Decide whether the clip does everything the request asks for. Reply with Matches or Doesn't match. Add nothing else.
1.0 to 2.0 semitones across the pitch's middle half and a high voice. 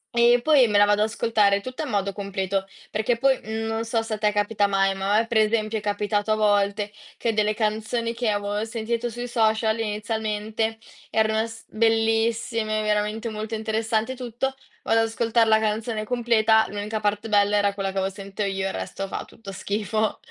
Matches